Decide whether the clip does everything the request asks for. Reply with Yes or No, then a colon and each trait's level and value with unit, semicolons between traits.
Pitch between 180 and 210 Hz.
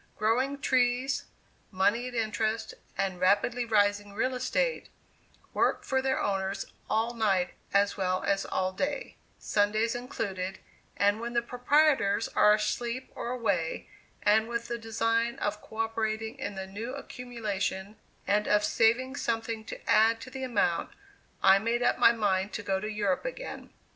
No: high, 220 Hz